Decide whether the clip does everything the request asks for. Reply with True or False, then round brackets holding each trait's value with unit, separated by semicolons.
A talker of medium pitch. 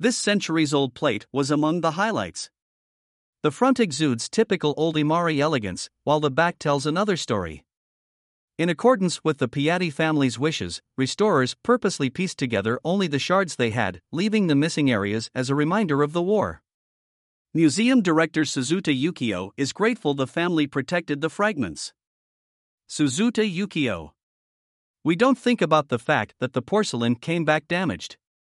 True (155 Hz)